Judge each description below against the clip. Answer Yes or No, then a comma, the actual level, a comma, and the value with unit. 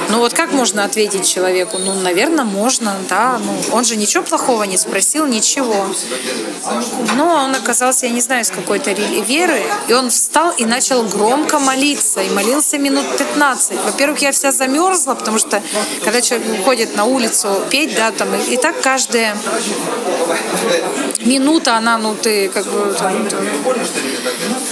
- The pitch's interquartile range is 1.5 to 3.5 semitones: No, average, 4.7 semitones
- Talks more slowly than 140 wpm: No, average, 155 wpm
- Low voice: No, high, 245 Hz